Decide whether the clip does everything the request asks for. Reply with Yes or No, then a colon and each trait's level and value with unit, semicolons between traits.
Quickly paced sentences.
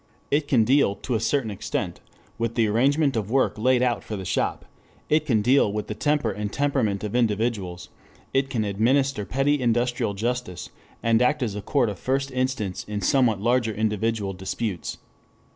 No: average, 175 wpm